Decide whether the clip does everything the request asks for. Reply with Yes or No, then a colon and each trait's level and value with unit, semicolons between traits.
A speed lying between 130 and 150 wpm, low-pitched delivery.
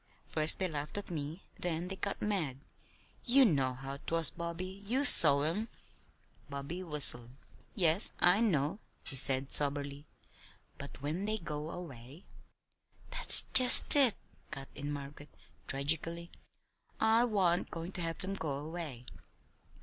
No: average, 140 wpm; medium, 165 Hz